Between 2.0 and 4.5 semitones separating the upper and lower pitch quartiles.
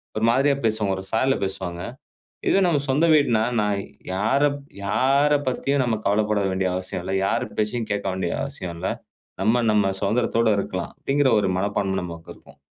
No: wide, 5.6 semitones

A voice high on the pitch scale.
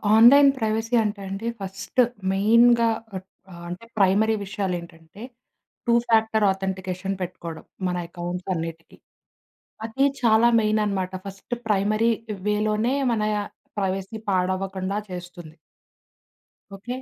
Yes: high, 195 Hz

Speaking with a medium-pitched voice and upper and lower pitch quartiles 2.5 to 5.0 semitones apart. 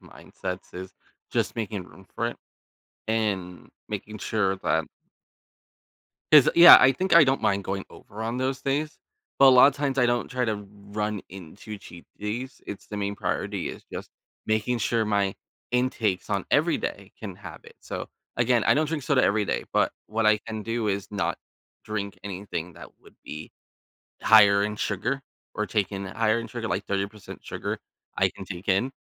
No: low, 110 Hz; average, 3.5 semitones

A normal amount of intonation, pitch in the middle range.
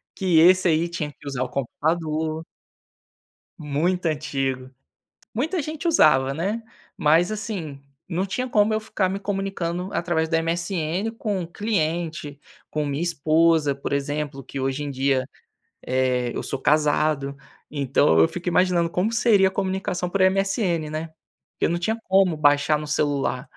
Yes: average, 4.5 semitones; medium, 165 Hz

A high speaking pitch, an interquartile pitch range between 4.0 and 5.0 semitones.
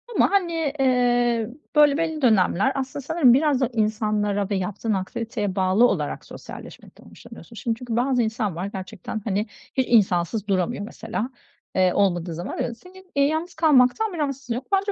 No: high, 235 Hz; wide, 5.4 semitones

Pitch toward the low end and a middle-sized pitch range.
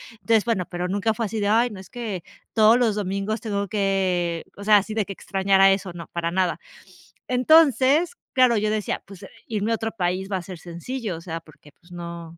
No: high, 200 Hz; average, 3.7 semitones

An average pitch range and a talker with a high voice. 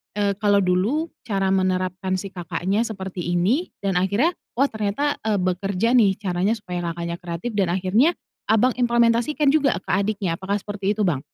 Yes: average, 3.9 semitones; high, 200 Hz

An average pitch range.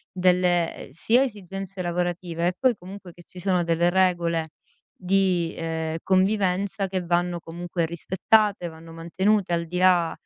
No: narrow, 1.9 semitones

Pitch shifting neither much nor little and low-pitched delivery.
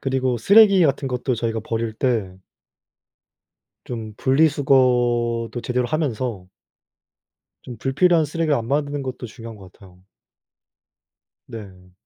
Yes: average, 3.8 semitones; low, 125 Hz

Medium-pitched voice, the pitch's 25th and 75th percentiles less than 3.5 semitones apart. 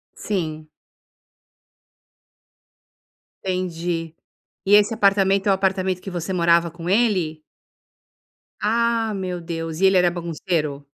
Yes: medium, 180 Hz; average, 2.9 semitones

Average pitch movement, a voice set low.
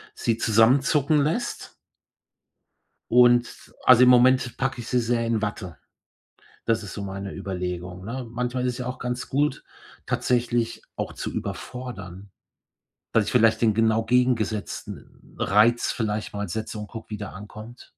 Yes: average, 3.0 semitones; low, 115 Hz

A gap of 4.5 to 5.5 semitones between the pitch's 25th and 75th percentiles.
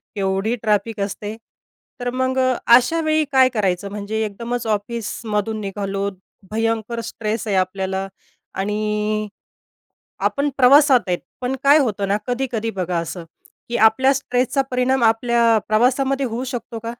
No: average, 3.5 semitones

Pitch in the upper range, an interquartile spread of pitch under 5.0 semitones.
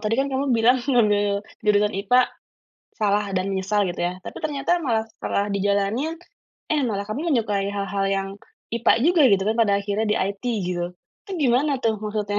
Yes: high, 210 Hz; average, 3.4 semitones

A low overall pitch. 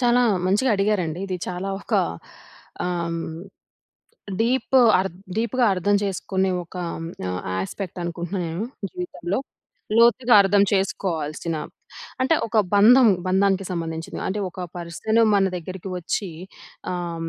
No: high, 190 Hz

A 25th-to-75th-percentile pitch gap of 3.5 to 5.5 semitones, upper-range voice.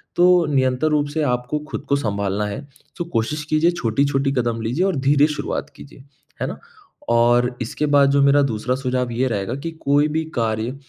No: average, 3.9 semitones; low, 135 Hz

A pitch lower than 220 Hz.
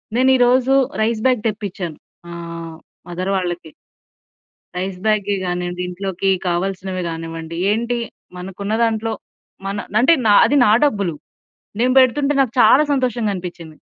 Yes: high, 200 Hz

